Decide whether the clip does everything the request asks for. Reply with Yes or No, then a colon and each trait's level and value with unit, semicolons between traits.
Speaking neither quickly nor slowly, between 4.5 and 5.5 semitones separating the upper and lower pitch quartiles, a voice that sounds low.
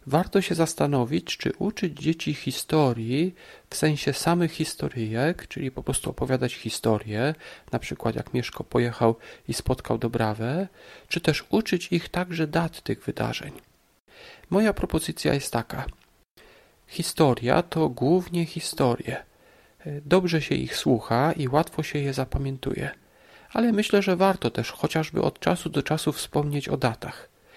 No: average, 135 wpm; average, 5.0 semitones; medium, 155 Hz